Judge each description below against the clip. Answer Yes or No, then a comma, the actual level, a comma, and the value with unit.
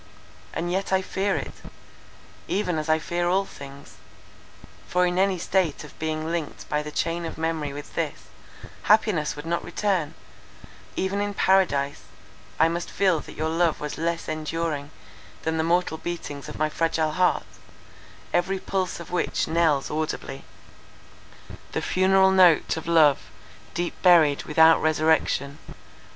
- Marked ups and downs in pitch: No, average, 2.8 semitones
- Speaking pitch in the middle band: Yes, medium, 165 Hz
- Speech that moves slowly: No, average, 145 wpm